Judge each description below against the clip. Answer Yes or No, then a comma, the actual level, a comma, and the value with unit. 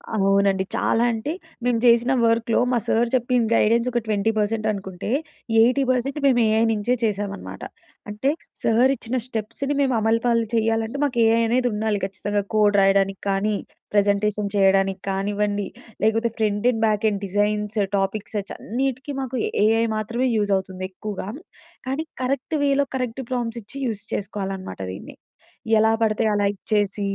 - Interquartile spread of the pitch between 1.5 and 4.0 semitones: Yes, average, 2.8 semitones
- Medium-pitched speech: No, high, 220 Hz